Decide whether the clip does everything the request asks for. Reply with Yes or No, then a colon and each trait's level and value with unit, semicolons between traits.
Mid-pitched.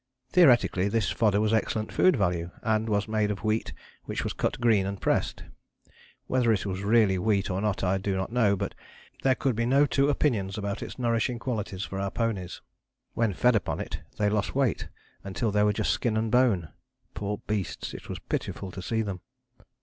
No: low, 105 Hz